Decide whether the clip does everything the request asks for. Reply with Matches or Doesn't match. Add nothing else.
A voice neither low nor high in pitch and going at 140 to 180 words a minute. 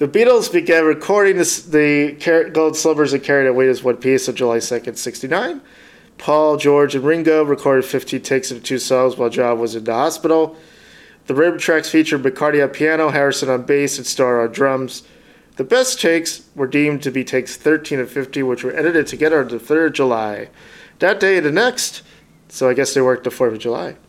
Doesn't match